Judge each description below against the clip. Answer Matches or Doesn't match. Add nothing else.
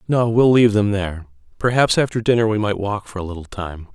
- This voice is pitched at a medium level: Doesn't match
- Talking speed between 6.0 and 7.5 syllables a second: Matches